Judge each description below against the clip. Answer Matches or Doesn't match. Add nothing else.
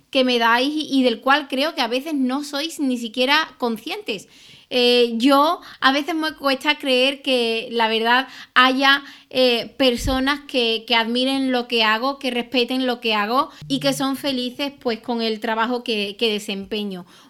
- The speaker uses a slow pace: Doesn't match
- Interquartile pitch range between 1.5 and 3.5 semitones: Matches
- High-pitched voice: Matches